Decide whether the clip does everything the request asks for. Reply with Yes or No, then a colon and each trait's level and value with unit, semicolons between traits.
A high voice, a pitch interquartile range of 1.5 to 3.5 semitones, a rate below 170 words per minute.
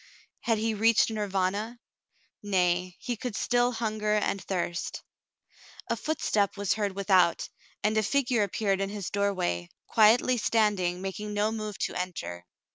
Yes: high, 205 Hz; average, 2.8 semitones; average, 140 wpm